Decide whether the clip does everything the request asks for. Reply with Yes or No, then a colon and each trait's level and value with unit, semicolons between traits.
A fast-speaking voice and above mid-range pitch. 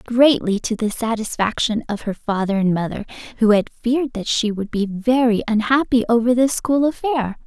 No: average, 175 wpm; high, 230 Hz